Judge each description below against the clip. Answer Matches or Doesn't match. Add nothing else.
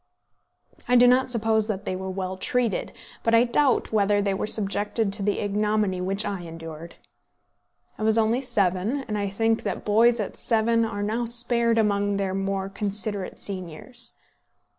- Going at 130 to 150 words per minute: Doesn't match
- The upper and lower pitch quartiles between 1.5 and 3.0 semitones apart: Matches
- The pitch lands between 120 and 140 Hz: Doesn't match